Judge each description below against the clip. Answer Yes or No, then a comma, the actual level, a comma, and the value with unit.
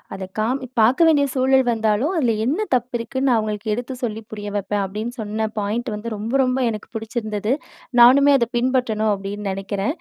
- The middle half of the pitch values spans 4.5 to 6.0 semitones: No, average, 3.3 semitones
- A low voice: No, high, 225 Hz